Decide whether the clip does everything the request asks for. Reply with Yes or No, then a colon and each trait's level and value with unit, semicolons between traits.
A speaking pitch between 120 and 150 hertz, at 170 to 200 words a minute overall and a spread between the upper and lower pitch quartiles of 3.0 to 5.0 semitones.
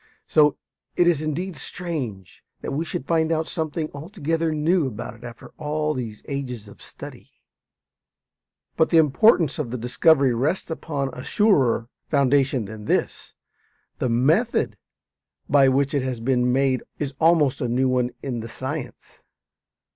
No: medium, 140 Hz; average, 150 wpm; average, 4.1 semitones